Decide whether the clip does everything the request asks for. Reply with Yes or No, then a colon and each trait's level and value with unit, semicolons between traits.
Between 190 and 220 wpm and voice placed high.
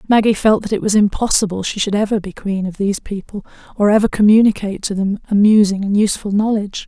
Yes: average, 200 wpm; high, 205 Hz